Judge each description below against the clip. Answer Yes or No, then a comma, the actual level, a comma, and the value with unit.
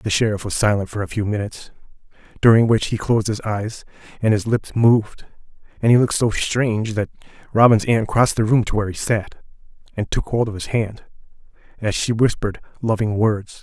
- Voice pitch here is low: Yes, low, 110 Hz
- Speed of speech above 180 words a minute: Yes, average, 195 wpm